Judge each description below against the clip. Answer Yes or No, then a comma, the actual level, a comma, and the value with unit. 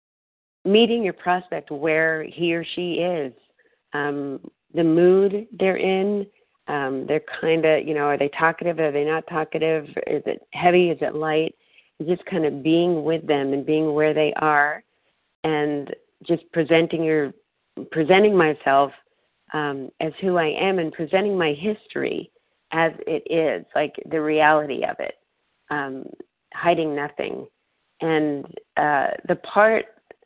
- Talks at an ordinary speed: Yes, average, 145 wpm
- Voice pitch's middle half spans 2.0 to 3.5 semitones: Yes, average, 2.9 semitones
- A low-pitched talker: No, medium, 160 Hz